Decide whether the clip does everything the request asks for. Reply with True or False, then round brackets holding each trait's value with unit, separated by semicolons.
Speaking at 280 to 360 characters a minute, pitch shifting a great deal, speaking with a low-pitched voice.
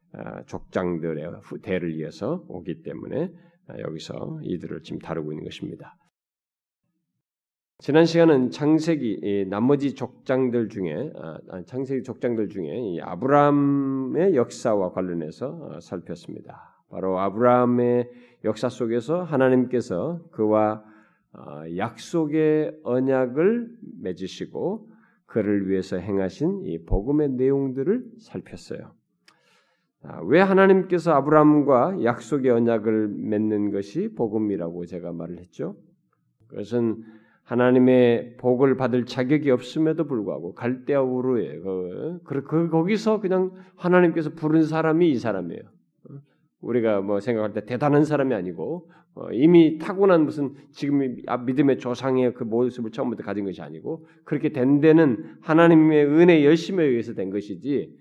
True (285 characters per minute; 6.7 semitones; 130 Hz)